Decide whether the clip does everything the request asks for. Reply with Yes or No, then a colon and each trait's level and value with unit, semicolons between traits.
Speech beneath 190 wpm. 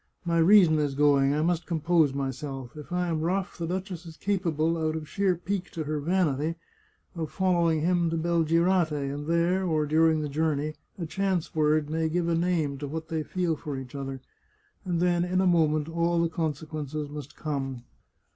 No: average, 195 wpm